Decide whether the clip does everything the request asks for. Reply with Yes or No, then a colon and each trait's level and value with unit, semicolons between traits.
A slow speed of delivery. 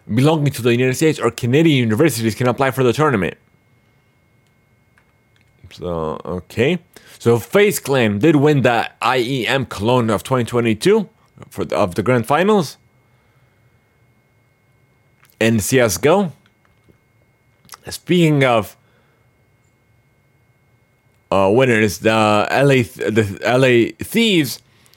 Yes: slow, 105 wpm